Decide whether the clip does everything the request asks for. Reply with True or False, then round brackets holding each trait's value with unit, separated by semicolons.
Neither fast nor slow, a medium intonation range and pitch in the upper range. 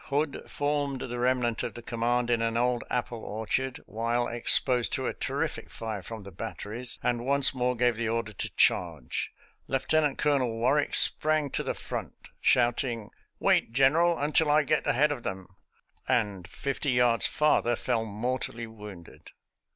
False (160 wpm; 3.0 semitones; 120 Hz)